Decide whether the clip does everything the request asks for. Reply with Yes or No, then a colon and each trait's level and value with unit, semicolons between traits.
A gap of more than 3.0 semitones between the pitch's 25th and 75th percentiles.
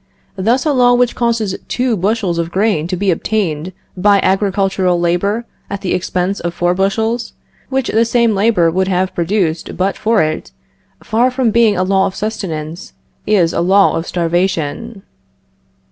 Yes: average, 4.0 semitones